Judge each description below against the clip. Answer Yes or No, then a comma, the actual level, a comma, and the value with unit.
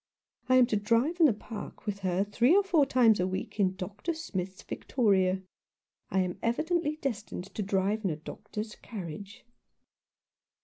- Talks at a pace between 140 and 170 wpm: Yes, average, 165 wpm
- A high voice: Yes, high, 210 Hz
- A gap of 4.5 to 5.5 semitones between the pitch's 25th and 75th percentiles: Yes, average, 5.2 semitones